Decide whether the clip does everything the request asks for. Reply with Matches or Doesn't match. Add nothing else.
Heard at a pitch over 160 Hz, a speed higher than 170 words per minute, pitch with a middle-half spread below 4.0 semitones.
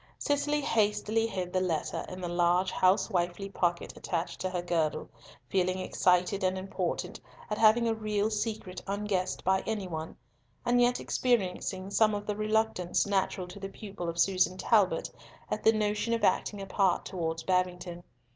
Doesn't match